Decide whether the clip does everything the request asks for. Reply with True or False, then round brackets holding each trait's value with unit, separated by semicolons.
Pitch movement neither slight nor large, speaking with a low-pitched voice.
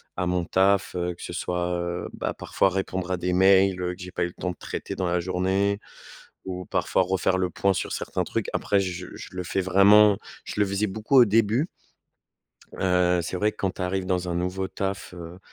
False (1.5 semitones; 95 Hz)